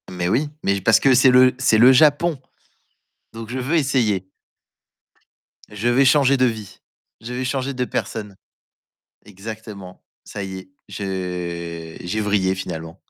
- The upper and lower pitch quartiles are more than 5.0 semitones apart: Yes, wide, 5.4 semitones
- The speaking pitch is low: Yes, low, 110 Hz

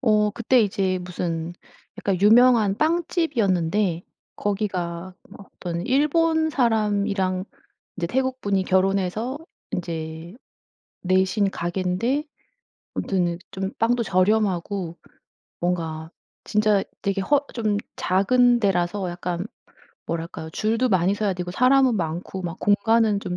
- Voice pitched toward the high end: Yes, high, 195 Hz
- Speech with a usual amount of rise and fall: Yes, average, 4.0 semitones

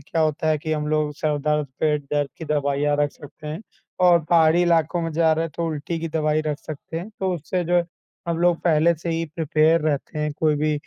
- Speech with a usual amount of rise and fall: No, narrow, 1.7 semitones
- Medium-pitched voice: Yes, medium, 155 Hz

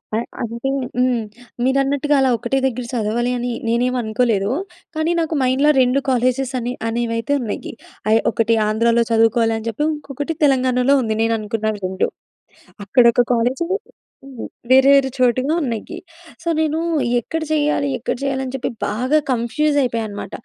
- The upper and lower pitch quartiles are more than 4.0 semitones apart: No, average, 3.0 semitones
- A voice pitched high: Yes, very high, 250 Hz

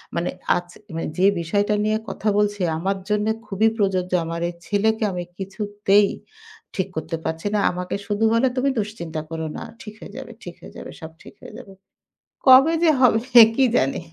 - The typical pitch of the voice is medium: No, high, 205 Hz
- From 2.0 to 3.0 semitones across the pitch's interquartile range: No, average, 3.5 semitones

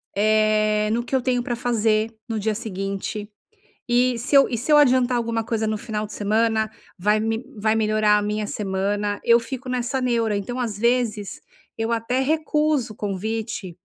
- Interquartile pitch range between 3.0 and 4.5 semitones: No, narrow, 2.4 semitones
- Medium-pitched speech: No, high, 225 Hz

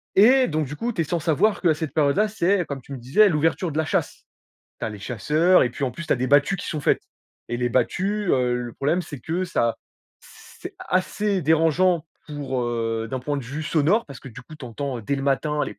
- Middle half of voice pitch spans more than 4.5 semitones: Yes, average, 5.3 semitones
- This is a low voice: No, medium, 150 Hz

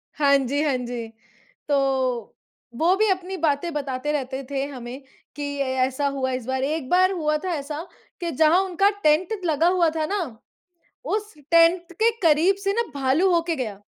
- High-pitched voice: Yes, very high, 300 Hz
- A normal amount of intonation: Yes, average, 4.7 semitones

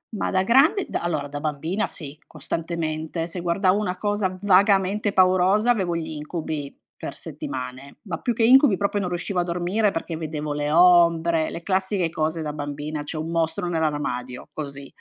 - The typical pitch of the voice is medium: Yes, medium, 170 Hz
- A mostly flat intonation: No, average, 3.8 semitones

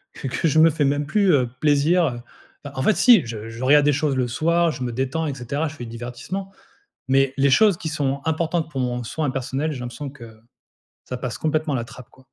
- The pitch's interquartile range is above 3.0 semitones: Yes, average, 4.1 semitones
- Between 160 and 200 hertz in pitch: No, medium, 140 Hz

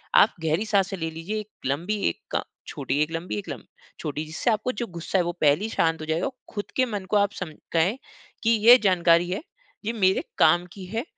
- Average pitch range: Yes, average, 4.6 semitones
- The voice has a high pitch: No, medium, 180 Hz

